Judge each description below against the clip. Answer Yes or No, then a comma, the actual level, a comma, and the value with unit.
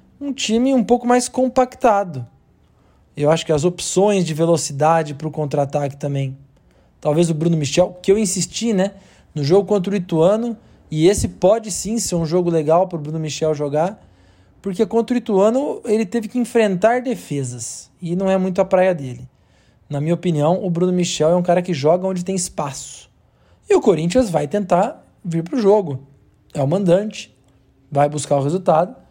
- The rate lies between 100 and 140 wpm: No, fast, 185 wpm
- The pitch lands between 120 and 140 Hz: No, medium, 175 Hz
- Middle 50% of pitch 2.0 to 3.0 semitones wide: No, wide, 5.6 semitones